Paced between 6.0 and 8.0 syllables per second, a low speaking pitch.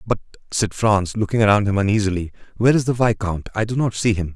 Yes: 6.1 syllables/s; low, 105 Hz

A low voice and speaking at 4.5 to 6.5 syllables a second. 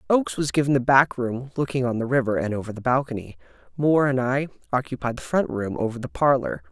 Yes: low, 125 Hz; 6.2 syllables/s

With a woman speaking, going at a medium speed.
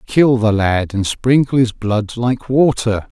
No: male; average, 170 wpm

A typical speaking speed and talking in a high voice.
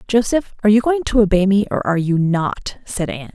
No: fast, 235 wpm; high, 205 Hz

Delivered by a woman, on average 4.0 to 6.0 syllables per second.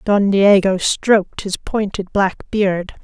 No: female; 3.5 syllables/s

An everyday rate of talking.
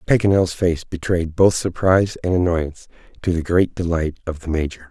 Yes: average, 170 wpm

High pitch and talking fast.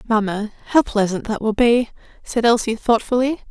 No: high, 225 Hz; average, 155 wpm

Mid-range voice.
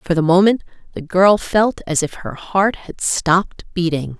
Yes: medium, 180 Hz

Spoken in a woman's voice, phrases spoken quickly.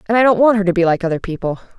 Yes: female; fast, 335 wpm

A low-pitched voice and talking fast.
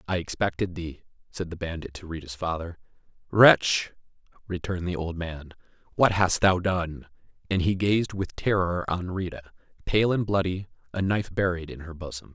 No: very low, 90 Hz; average, 160 wpm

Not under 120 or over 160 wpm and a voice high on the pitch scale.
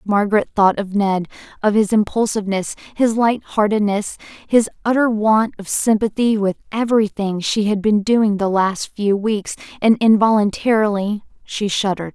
Yes: average, 145 wpm; high, 210 Hz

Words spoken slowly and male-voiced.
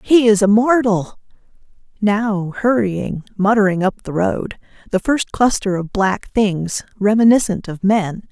No: slow, 130 wpm; female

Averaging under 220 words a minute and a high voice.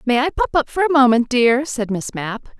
No: fast, 255 wpm; very high, 250 Hz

